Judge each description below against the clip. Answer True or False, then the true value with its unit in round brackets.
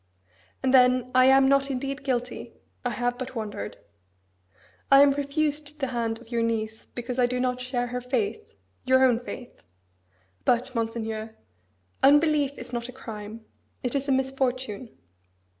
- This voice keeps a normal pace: True (155 wpm)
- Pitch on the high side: True (250 Hz)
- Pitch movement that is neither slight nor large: False (2.3 semitones)